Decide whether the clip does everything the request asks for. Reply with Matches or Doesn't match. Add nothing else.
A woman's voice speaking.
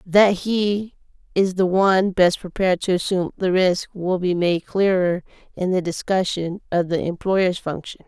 Matches